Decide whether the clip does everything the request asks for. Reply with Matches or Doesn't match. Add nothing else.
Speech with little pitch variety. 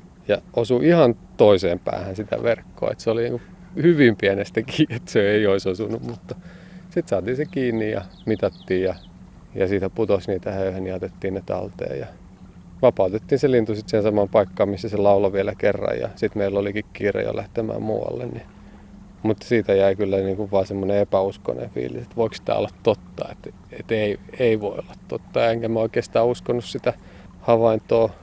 Doesn't match